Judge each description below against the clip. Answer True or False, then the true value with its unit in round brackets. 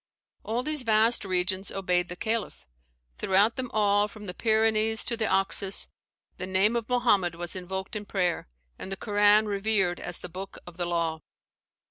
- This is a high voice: True (200 Hz)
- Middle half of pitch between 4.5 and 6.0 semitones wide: False (3.2 semitones)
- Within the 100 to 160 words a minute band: False (170 wpm)